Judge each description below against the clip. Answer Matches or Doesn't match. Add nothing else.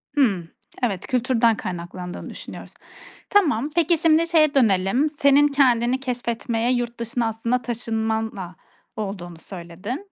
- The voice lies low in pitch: Doesn't match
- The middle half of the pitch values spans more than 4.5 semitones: Matches